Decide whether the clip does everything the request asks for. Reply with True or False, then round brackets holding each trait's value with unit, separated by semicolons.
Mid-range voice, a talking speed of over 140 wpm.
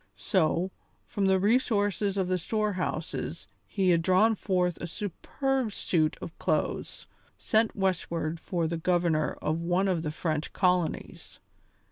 False (180 Hz; 135 wpm)